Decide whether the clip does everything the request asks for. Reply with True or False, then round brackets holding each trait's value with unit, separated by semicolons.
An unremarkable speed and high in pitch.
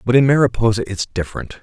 False (185 wpm; 115 Hz)